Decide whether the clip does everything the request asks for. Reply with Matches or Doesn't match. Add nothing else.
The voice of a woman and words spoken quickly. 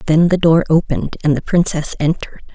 Doesn't match